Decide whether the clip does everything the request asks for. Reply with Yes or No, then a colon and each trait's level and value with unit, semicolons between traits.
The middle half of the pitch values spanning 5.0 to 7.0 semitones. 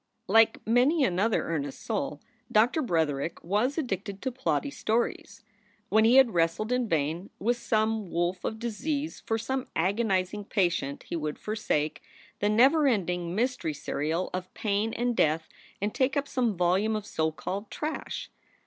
Yes: wide, 5.6 semitones